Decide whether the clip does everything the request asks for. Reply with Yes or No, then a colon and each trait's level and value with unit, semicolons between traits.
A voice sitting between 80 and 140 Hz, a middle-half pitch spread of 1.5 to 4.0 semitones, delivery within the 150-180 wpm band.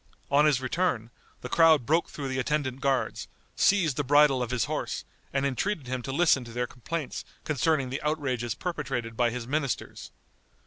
Yes: low, 135 Hz; average, 3.5 semitones; average, 175 wpm